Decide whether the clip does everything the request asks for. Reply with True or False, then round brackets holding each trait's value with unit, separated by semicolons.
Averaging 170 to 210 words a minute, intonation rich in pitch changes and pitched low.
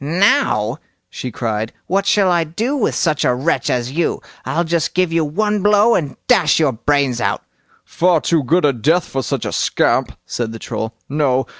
False (190 wpm; 6.1 semitones; 155 Hz)